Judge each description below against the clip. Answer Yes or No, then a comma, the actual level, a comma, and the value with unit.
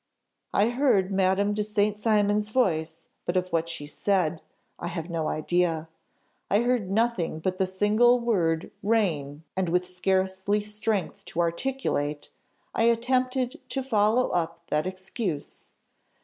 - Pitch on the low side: No, high, 190 Hz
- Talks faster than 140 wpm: No, slow, 135 wpm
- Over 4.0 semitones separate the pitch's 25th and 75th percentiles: Yes, average, 4.7 semitones